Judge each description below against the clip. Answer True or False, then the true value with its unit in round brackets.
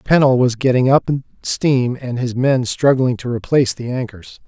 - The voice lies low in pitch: True (125 Hz)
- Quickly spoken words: False (175 wpm)